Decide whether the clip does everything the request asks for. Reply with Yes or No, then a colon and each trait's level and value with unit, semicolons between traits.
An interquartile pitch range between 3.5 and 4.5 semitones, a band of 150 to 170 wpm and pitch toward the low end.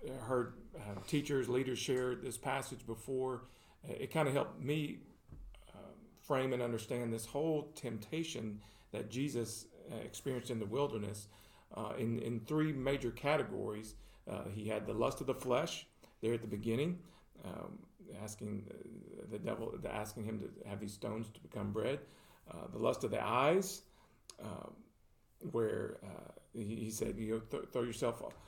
Yes: average, 3.9 semitones; average, 165 wpm; low, 120 Hz